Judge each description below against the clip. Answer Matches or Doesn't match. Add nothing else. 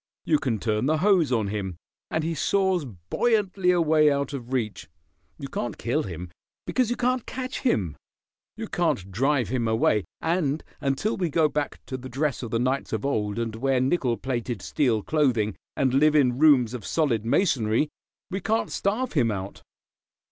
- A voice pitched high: Doesn't match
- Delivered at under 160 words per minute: Doesn't match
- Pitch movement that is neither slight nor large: Doesn't match